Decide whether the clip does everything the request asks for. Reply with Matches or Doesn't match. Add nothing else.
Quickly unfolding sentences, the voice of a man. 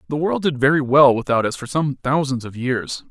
Matches